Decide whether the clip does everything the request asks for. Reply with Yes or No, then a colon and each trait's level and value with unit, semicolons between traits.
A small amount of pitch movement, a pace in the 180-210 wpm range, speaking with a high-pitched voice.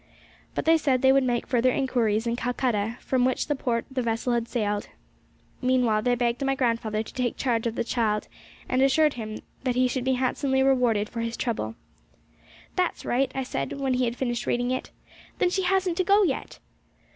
Yes: narrow, 2.3 semitones; average, 190 wpm; very high, 250 Hz